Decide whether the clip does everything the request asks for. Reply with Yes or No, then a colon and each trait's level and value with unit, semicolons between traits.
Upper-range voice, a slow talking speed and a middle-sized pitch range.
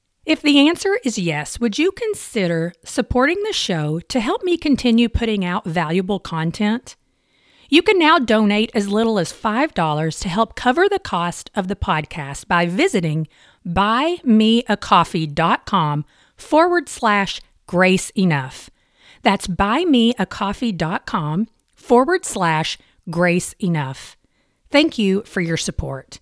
No: high, 205 Hz; slow, 120 wpm; wide, 6.4 semitones